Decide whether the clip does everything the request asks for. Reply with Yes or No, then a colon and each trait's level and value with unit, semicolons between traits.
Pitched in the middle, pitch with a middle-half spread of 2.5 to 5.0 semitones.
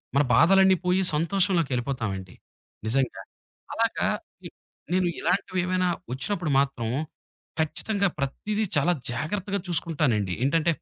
No: medium, 165 Hz; wide, 5.6 semitones